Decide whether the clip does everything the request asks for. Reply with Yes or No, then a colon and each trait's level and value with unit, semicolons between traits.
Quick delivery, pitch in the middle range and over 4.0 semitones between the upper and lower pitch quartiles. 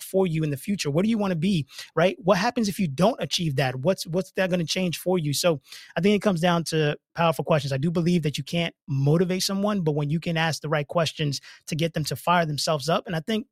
No: fast, 275 wpm; medium, 170 Hz; average, 3.1 semitones